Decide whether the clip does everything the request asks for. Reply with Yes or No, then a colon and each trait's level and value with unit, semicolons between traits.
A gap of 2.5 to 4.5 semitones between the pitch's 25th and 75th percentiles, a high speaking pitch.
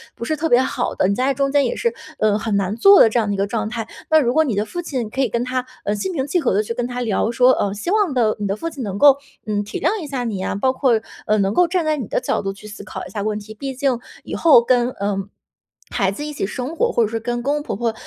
No: average, 5.2 semitones; high, 240 Hz